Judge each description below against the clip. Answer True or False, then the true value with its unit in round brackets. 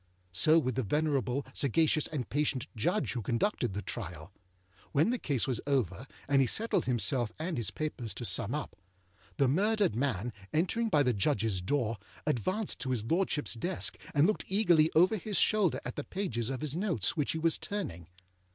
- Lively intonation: True (6.0 semitones)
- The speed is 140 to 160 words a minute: False (180 wpm)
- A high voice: False (140 Hz)